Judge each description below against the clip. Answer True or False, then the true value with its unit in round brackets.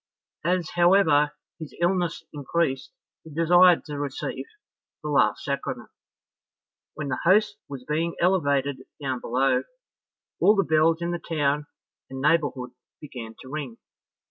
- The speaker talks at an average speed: False (130 wpm)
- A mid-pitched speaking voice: True (155 Hz)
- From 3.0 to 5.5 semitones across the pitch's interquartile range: True (3.7 semitones)